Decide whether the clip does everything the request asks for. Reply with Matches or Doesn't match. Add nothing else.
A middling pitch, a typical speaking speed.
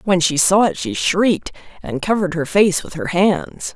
Doesn't match